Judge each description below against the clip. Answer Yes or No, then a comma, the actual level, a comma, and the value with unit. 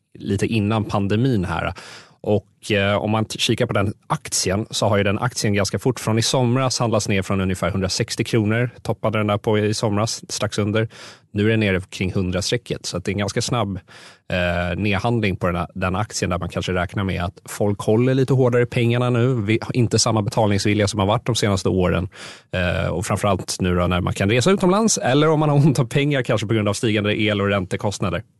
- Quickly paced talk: Yes, fast, 220 wpm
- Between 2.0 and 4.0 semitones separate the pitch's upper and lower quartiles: Yes, average, 3.3 semitones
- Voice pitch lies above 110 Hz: No, low, 105 Hz